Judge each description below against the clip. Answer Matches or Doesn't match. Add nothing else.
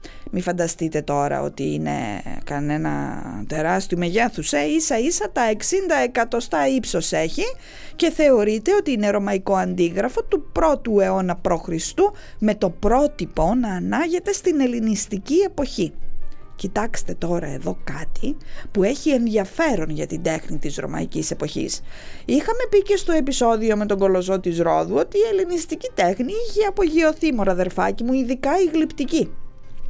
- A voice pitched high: Matches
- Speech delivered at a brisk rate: Doesn't match